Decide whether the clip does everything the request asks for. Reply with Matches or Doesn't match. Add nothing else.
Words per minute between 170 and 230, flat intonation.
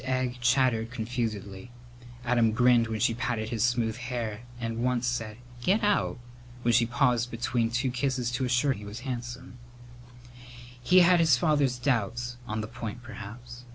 Doesn't match